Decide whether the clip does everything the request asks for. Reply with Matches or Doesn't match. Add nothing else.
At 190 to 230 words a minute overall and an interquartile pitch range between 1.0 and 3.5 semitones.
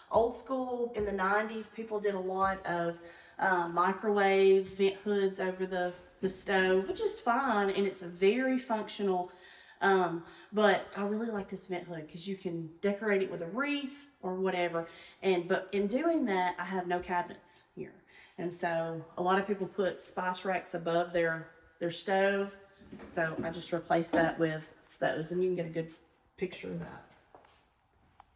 Doesn't match